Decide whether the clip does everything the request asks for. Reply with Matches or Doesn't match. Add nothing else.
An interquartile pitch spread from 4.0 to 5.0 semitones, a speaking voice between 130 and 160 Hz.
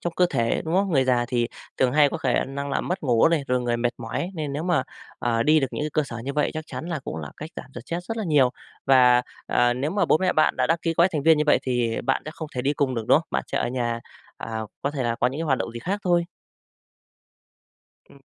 Matches